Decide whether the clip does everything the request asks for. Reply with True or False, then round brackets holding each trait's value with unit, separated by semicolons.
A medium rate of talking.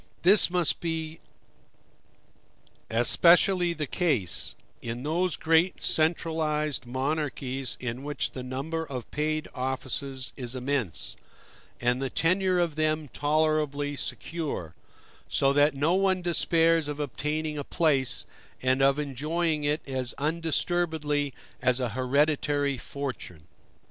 False (115 wpm)